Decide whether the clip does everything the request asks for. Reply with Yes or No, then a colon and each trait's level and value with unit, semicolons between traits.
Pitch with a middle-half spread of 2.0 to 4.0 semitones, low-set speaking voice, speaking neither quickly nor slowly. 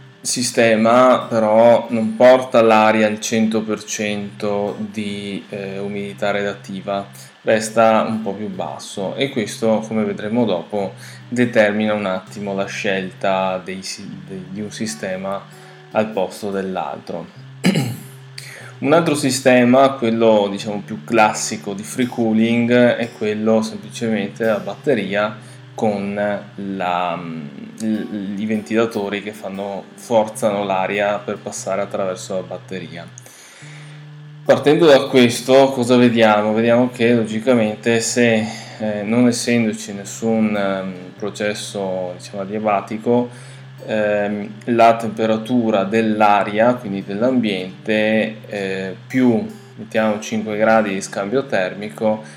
No: average, 2.9 semitones; low, 110 Hz; slow, 105 wpm